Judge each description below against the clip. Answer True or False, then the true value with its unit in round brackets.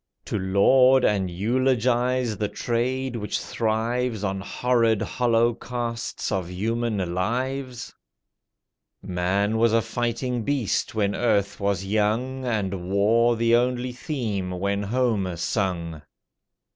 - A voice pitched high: False (115 Hz)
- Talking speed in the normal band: False (110 wpm)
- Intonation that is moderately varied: True (3.7 semitones)